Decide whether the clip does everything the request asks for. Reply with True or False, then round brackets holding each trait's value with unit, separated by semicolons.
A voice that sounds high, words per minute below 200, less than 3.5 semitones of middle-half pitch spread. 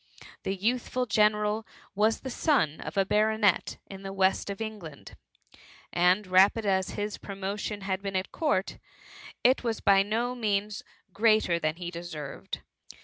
True (200 Hz; 150 wpm; 2.5 semitones)